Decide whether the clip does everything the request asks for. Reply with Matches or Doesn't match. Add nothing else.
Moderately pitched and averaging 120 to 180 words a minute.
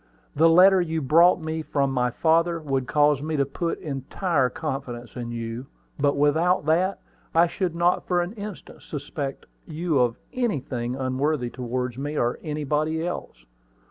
Matches